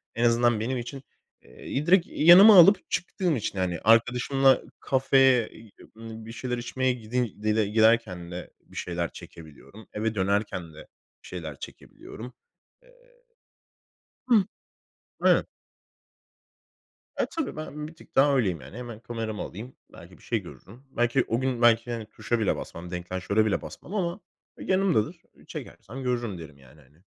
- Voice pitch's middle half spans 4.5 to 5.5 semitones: Yes, average, 4.9 semitones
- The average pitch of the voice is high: No, low, 115 Hz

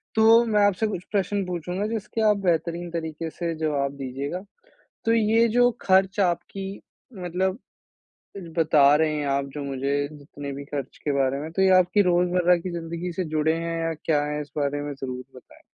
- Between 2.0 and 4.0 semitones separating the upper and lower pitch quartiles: No, average, 4.7 semitones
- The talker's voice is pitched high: No, medium, 165 Hz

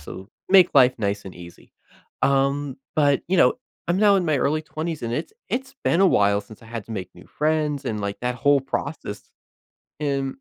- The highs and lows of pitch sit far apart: Yes, wide, 6.2 semitones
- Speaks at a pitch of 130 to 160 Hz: Yes, medium, 140 Hz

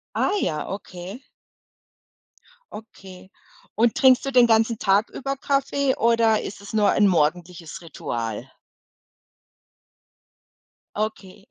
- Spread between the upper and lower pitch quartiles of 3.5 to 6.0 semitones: Yes, average, 4.6 semitones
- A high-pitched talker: Yes, high, 210 Hz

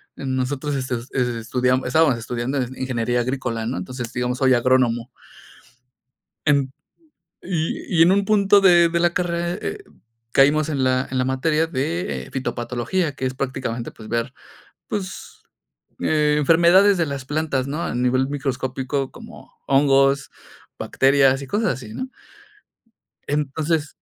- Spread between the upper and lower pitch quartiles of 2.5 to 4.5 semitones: Yes, average, 3.9 semitones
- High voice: No, low, 135 Hz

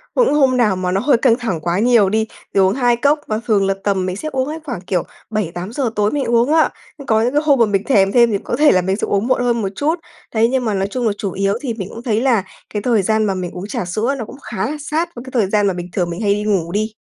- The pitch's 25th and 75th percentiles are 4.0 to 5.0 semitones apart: Yes, average, 4.3 semitones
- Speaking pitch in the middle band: No, high, 220 Hz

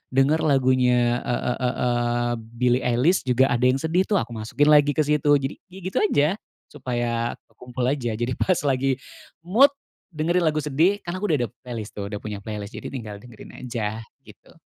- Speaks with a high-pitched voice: No, low, 130 Hz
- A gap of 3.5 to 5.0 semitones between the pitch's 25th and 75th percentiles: Yes, average, 3.9 semitones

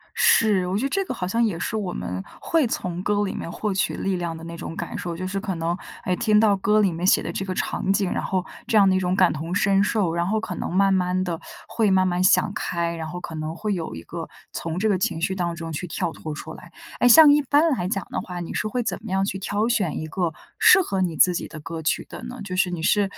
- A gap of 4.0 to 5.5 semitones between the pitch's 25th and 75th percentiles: No, average, 3.3 semitones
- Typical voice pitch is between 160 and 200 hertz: Yes, medium, 185 Hz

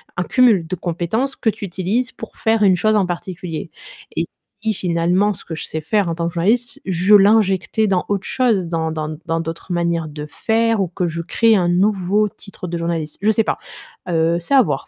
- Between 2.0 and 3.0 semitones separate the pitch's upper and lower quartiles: No, average, 4.1 semitones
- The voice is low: No, medium, 180 Hz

